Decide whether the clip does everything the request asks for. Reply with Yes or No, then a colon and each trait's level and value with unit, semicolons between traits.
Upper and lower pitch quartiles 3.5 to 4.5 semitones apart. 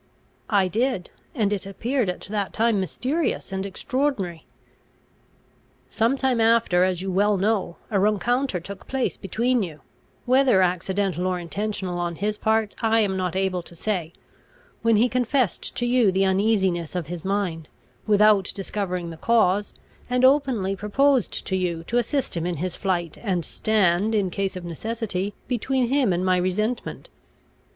Yes: average, 4.1 semitones